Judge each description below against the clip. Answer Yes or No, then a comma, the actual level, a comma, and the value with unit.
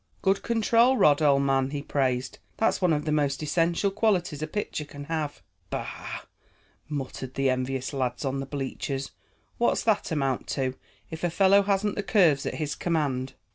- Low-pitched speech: No, medium, 150 Hz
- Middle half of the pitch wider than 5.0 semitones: Yes, wide, 5.5 semitones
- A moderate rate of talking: Yes, average, 175 wpm